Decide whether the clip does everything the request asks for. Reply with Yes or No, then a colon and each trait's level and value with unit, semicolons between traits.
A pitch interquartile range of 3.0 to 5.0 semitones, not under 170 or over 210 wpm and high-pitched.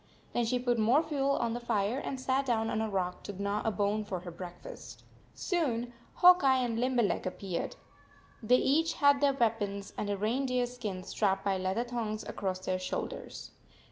Yes: average, 4.2 semitones; average, 190 wpm; high, 225 Hz